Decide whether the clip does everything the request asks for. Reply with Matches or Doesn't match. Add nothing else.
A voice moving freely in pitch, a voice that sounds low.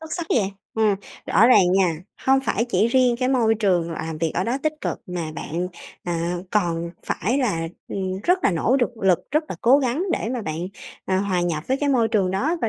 Doesn't match